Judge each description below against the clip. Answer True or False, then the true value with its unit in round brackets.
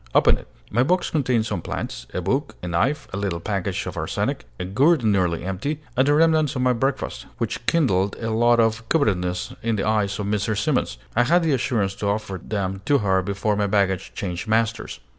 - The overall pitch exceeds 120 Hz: False (110 Hz)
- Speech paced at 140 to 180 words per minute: False (205 wpm)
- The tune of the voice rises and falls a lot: False (5.0 semitones)